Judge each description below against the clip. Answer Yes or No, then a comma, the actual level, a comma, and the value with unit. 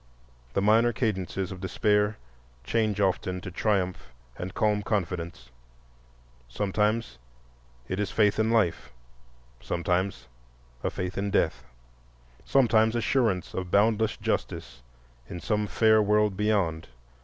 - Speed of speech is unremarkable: No, slow, 115 wpm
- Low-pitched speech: Yes, low, 105 Hz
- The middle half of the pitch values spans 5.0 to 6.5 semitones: No, average, 3.0 semitones